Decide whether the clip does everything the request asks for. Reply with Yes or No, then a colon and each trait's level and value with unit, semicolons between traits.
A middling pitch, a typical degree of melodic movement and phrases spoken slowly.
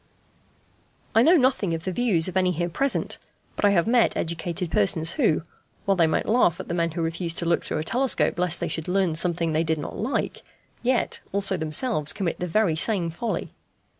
No: medium, 175 Hz; average, 4.3 semitones; fast, 205 wpm